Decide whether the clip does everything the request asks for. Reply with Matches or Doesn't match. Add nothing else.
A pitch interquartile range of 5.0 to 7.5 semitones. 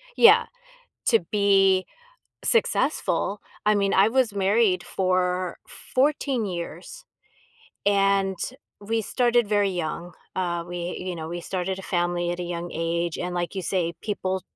Doesn't match